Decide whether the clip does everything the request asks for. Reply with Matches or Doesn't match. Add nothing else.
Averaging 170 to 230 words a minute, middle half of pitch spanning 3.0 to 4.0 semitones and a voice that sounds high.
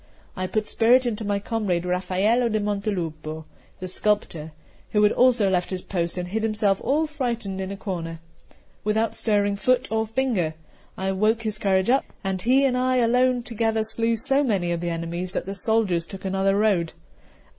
Matches